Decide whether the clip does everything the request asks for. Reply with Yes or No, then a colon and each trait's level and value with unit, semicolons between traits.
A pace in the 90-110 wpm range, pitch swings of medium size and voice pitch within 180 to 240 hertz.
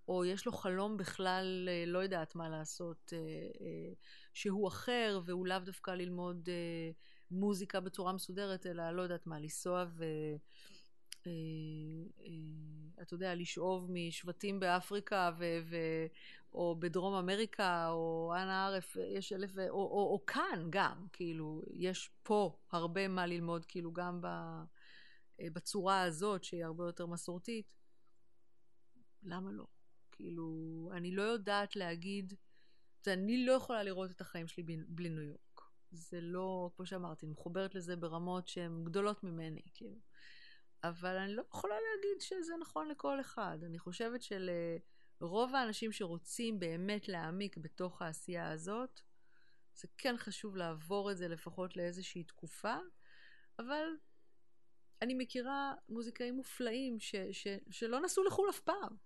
No: average, 130 wpm; average, 3.3 semitones; medium, 185 Hz